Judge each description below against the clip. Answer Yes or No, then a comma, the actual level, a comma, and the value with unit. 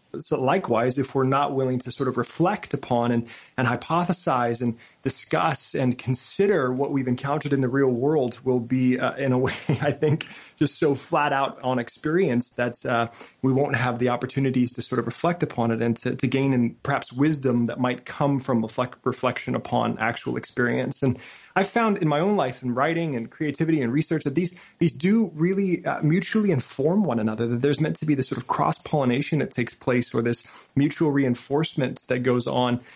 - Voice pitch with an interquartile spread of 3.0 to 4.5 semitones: Yes, average, 3.6 semitones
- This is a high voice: No, low, 135 Hz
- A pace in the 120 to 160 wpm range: No, average, 200 wpm